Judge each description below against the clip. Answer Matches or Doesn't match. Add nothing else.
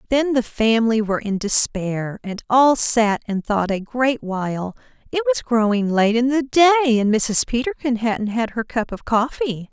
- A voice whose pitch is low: Doesn't match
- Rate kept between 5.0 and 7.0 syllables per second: Doesn't match